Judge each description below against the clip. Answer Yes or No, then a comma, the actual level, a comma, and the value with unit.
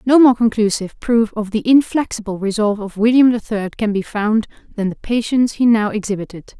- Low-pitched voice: No, high, 220 Hz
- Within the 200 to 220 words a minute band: No, average, 190 wpm